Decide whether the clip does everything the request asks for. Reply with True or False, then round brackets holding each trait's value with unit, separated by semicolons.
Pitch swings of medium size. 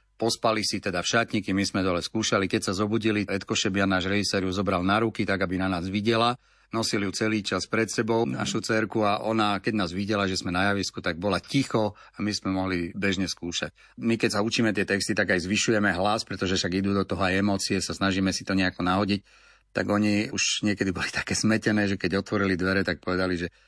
False (2.3 semitones)